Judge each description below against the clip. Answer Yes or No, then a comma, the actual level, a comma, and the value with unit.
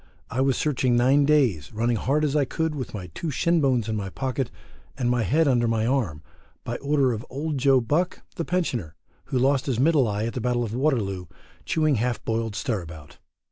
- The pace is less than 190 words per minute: No, fast, 205 wpm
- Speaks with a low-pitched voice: Yes, low, 125 Hz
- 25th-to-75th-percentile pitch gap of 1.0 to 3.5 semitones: No, average, 4.2 semitones